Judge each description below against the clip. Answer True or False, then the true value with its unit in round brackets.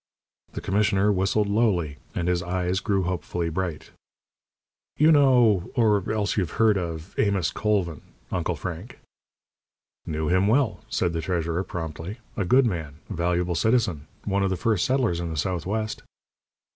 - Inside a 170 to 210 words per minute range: False (150 wpm)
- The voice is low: True (95 Hz)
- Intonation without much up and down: False (3.8 semitones)